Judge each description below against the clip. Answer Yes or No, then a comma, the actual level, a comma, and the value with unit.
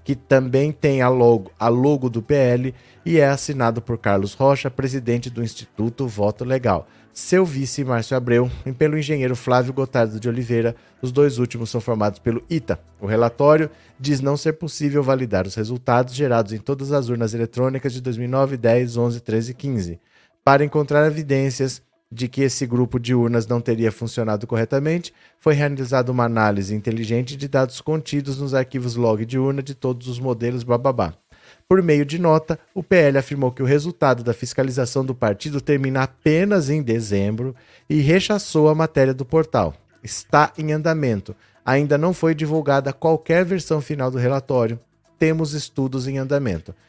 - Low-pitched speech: Yes, low, 130 Hz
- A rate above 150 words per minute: Yes, average, 170 wpm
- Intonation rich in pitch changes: No, average, 3.6 semitones